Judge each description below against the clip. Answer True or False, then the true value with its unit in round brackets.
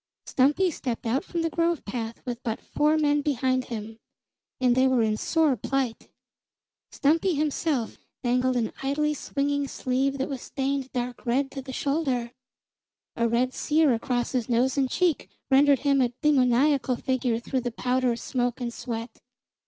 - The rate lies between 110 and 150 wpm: False (160 wpm)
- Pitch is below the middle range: False (260 Hz)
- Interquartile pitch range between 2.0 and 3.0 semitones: True (2.7 semitones)